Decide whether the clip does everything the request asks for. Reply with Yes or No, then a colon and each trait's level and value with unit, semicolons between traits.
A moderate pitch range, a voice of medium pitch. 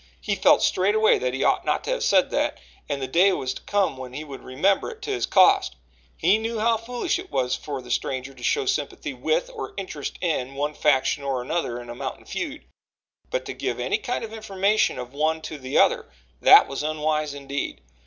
No: wide, 8.6 semitones; medium, 155 Hz